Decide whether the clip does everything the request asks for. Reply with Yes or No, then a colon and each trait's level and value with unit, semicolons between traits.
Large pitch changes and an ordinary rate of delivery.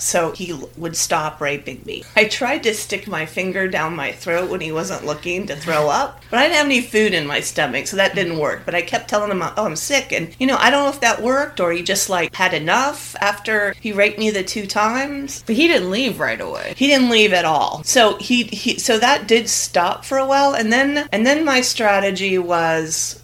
No: wide, 5.8 semitones; fast, 240 wpm